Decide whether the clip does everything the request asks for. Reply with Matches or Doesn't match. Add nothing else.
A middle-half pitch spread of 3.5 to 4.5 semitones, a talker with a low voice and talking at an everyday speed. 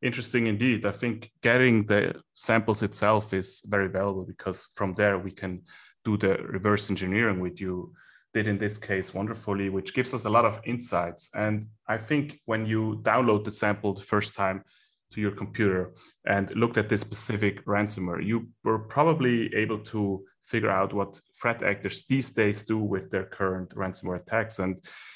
Doesn't match